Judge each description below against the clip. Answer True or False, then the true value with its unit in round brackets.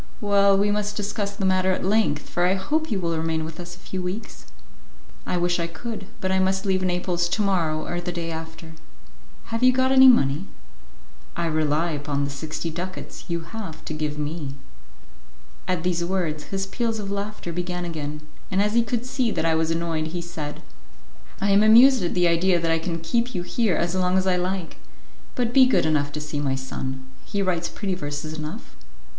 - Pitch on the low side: False (180 Hz)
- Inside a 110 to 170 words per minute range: False (205 wpm)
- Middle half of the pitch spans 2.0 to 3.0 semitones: False (3.7 semitones)